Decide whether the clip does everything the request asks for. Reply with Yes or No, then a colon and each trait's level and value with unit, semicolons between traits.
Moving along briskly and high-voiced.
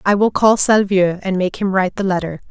Yes: fast, 240 wpm; high, 195 Hz